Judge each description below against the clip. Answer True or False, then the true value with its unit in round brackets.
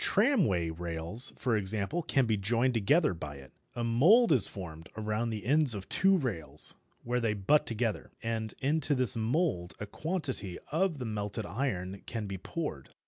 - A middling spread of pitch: False (6.3 semitones)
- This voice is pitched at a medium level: False (115 Hz)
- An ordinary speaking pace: True (170 wpm)